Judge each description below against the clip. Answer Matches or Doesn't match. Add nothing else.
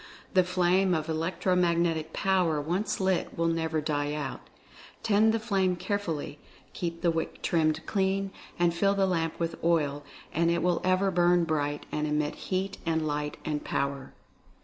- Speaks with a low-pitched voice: Doesn't match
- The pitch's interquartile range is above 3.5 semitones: Doesn't match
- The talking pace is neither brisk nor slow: Matches